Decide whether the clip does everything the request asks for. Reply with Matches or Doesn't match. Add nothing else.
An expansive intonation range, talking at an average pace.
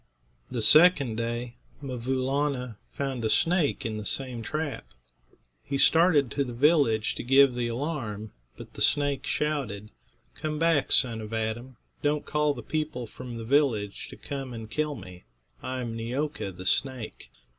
Doesn't match